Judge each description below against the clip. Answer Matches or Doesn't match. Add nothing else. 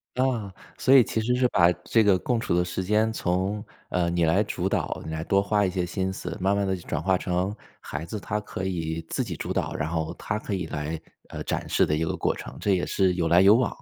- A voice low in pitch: Matches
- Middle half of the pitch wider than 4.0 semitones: Doesn't match